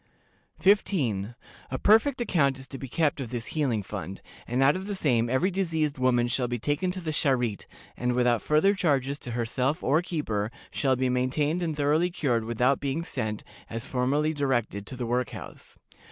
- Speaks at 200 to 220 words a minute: No, average, 185 wpm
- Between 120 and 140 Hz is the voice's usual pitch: Yes, low, 135 Hz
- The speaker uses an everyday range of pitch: Yes, average, 4.4 semitones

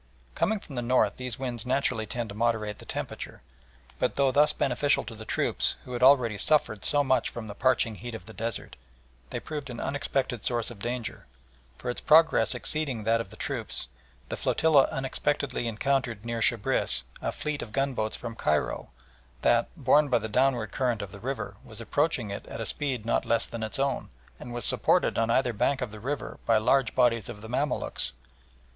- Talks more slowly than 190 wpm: No, average, 195 wpm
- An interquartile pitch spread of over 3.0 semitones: Yes, average, 3.4 semitones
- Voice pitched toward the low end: Yes, low, 120 Hz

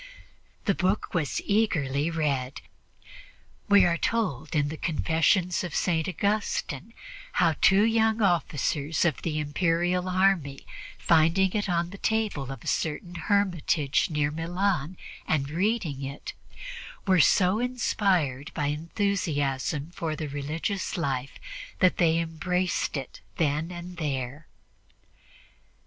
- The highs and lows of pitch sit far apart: No, average, 4.2 semitones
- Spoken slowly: Yes, slow, 120 wpm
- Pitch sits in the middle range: Yes, medium, 165 Hz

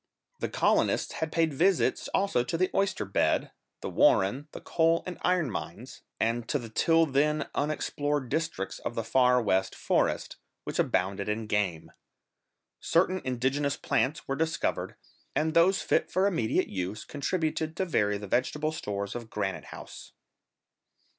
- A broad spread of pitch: Yes, wide, 7.0 semitones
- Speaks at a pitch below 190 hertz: Yes, medium, 140 Hz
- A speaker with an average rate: Yes, average, 150 wpm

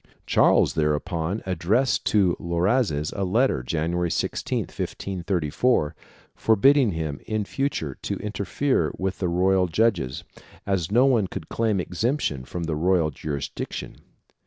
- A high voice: No, very low, 90 Hz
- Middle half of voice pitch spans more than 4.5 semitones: Yes, average, 5.1 semitones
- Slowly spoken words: Yes, slow, 125 wpm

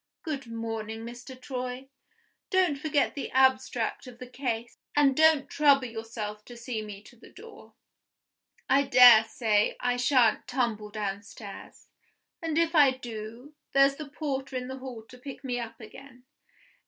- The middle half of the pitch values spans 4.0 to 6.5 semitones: No, average, 3.4 semitones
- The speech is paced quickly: No, average, 155 wpm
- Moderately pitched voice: No, very high, 250 Hz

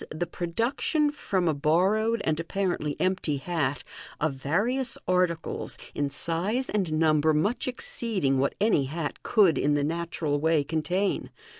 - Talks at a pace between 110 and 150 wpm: Yes, average, 140 wpm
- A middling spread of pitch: Yes, average, 4.9 semitones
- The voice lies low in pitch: No, medium, 165 Hz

